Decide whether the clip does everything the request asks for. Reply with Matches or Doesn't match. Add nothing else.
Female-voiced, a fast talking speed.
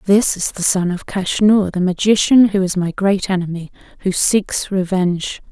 Doesn't match